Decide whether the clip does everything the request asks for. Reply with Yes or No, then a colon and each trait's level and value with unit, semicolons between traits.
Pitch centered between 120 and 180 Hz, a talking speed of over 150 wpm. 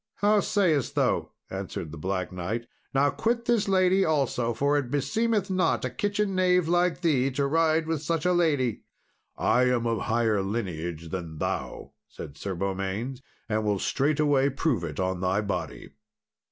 Yes: low, 135 Hz; average, 165 wpm